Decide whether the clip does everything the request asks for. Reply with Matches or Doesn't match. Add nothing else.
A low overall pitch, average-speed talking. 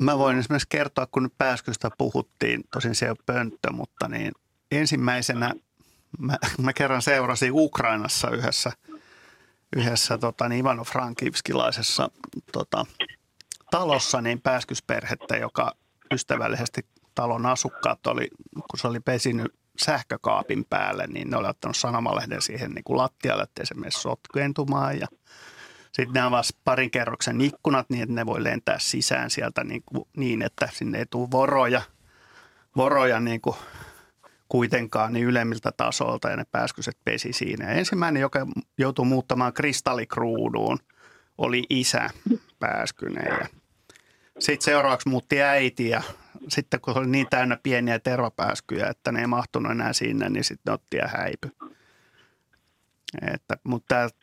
Matches